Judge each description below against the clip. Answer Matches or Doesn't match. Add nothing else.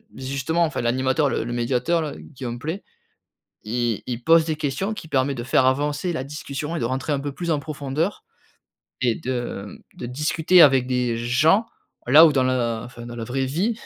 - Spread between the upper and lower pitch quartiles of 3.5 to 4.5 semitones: Matches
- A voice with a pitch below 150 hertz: Matches